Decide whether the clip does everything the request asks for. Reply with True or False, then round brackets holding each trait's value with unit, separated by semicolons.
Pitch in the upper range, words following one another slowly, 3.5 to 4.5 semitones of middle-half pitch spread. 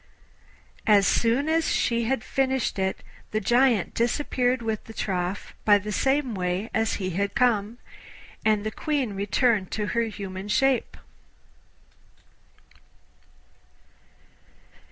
True (220 Hz; 115 wpm; 3.8 semitones)